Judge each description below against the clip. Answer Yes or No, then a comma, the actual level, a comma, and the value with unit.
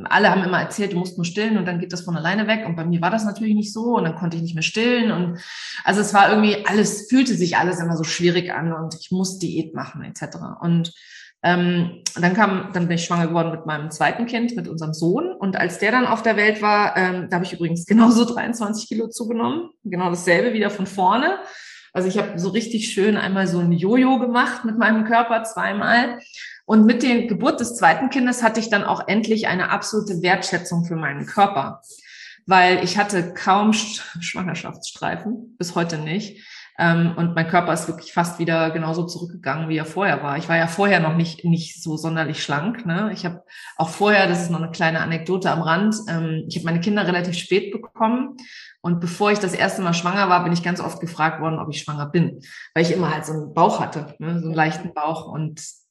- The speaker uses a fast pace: Yes, fast, 215 wpm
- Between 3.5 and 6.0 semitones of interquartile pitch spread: Yes, average, 4.1 semitones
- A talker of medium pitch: Yes, medium, 180 Hz